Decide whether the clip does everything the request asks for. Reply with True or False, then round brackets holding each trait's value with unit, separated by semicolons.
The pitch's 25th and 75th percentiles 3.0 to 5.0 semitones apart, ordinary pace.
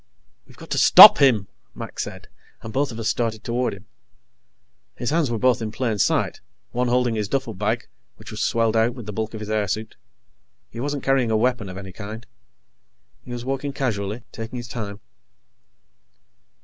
False (2.6 semitones; 180 wpm)